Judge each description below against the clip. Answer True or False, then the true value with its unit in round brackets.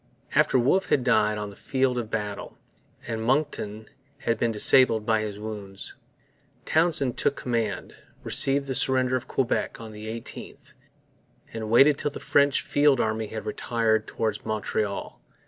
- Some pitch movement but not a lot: True (3.4 semitones)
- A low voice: True (115 Hz)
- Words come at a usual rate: True (150 wpm)